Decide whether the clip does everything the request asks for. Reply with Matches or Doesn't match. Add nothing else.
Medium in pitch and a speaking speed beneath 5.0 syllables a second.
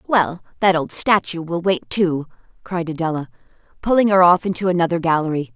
Doesn't match